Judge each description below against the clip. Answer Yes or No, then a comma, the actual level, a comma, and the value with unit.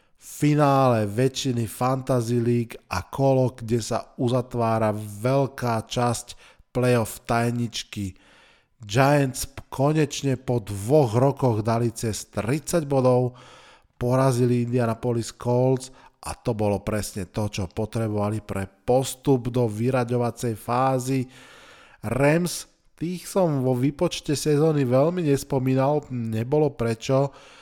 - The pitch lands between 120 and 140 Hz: Yes, low, 125 Hz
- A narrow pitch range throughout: No, average, 3.1 semitones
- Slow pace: Yes, slow, 100 wpm